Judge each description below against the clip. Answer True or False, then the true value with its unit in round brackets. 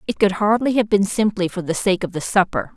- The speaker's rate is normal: False (260 wpm)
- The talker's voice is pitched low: False (195 Hz)